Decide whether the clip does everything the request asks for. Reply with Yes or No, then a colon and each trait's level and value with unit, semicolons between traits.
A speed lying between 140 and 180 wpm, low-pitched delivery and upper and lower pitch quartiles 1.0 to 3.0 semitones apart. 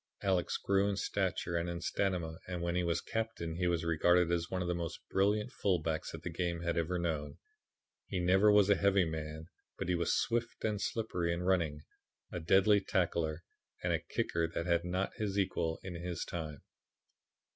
No: average, 190 wpm; very low, 85 Hz; narrow, 2.5 semitones